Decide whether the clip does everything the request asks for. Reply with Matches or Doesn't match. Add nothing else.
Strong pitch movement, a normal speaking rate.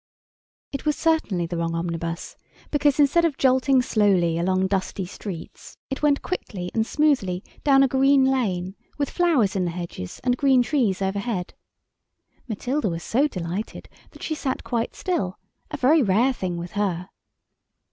Matches